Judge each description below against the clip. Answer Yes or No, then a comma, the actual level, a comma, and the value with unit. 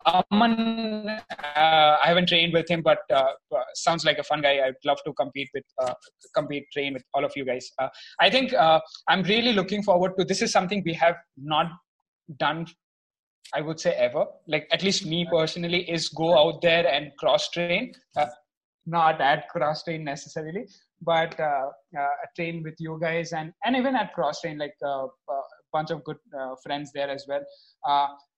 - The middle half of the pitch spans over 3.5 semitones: Yes, average, 4.4 semitones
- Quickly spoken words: No, average, 190 wpm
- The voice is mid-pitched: Yes, medium, 165 Hz